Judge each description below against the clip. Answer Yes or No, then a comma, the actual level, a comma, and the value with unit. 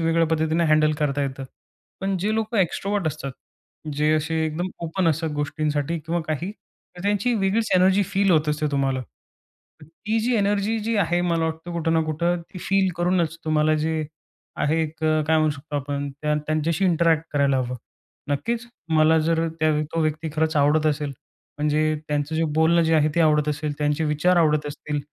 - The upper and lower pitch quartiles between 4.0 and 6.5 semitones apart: No, narrow, 2.5 semitones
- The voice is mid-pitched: Yes, medium, 160 Hz